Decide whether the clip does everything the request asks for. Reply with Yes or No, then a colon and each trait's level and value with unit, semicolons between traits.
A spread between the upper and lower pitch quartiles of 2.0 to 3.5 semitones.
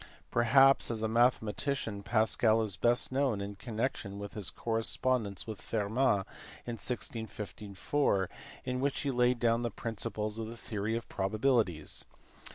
Yes: average, 2.8 semitones